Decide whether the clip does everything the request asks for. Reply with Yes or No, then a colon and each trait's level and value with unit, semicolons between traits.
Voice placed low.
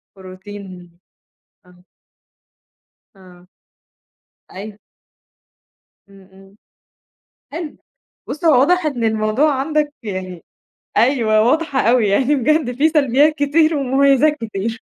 No: high, 245 Hz